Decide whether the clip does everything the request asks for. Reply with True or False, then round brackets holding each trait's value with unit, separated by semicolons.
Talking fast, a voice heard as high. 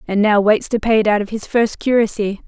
True (265 wpm; 215 Hz)